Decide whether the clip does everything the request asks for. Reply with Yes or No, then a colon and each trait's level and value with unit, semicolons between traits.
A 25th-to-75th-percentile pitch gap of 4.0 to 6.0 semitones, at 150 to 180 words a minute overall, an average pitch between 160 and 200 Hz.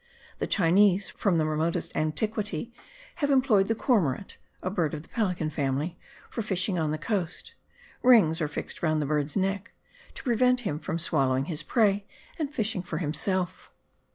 Yes: wide, 5.4 semitones; average, 165 wpm; medium, 185 Hz